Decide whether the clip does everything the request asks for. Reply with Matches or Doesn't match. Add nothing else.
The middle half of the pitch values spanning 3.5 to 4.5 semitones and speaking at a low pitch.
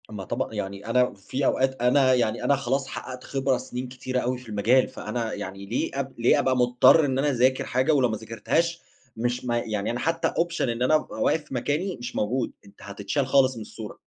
Doesn't match